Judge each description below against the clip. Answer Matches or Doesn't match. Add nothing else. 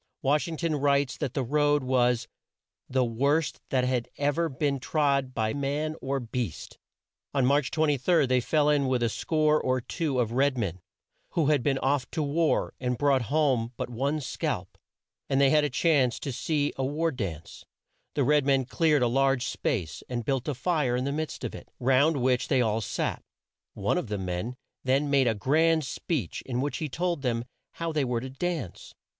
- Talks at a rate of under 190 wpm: Doesn't match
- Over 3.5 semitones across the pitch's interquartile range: Doesn't match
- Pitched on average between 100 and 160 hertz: Matches